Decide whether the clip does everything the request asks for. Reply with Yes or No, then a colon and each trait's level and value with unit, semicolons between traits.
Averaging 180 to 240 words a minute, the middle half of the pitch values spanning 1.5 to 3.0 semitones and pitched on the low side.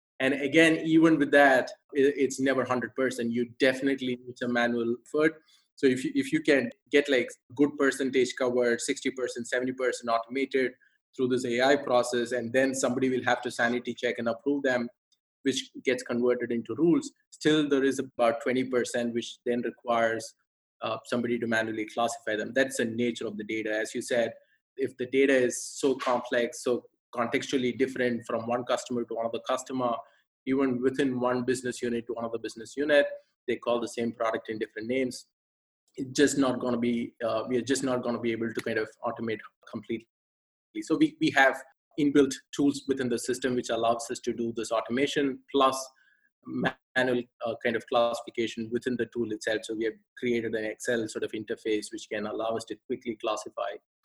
Yes: average, 185 wpm; narrow, 2.4 semitones; low, 125 Hz